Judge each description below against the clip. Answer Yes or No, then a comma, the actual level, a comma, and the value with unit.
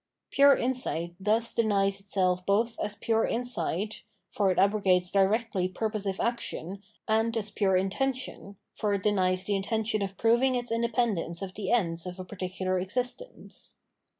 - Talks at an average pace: Yes, average, 150 wpm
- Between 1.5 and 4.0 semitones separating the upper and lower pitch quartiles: Yes, average, 3.5 semitones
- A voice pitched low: No, high, 205 Hz